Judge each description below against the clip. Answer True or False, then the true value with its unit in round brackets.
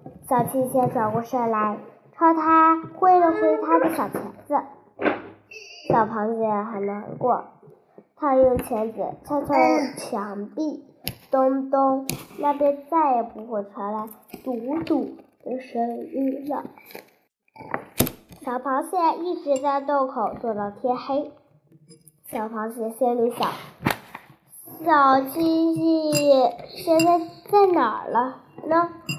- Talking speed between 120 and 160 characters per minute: True (155 characters per minute)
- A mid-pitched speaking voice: False (265 Hz)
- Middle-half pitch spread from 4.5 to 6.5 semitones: True (5.5 semitones)